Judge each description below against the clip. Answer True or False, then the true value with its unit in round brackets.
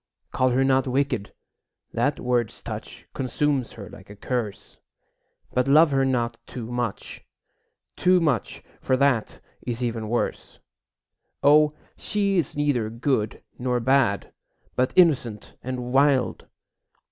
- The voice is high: False (125 Hz)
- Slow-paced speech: True (125 wpm)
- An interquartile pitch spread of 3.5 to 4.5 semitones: False (3.1 semitones)